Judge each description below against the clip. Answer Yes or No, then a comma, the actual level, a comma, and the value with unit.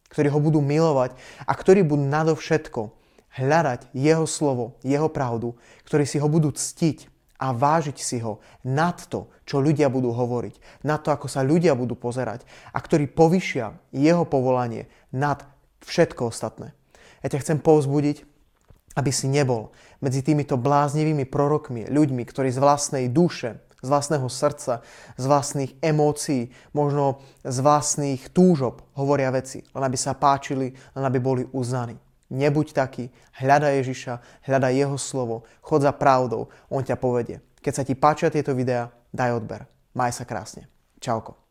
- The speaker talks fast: No, average, 150 wpm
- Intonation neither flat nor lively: Yes, average, 3.1 semitones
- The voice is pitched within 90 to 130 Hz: No, medium, 140 Hz